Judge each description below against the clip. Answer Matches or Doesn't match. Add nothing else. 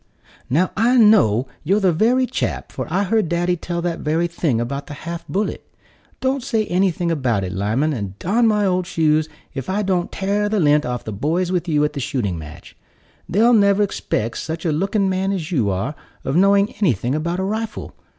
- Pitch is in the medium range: Matches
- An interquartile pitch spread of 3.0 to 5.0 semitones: Doesn't match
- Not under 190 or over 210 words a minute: Matches